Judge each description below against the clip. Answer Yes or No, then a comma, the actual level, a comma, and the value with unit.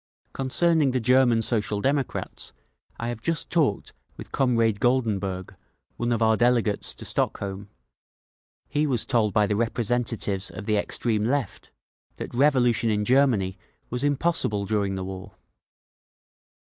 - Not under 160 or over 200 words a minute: No, slow, 135 wpm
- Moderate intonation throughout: Yes, average, 3.9 semitones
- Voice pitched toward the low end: Yes, low, 115 Hz